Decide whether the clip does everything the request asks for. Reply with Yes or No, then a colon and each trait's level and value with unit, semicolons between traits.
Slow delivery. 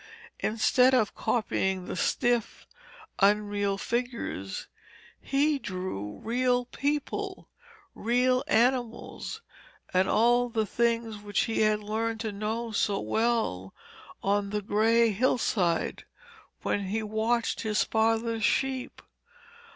Yes: slow, 105 wpm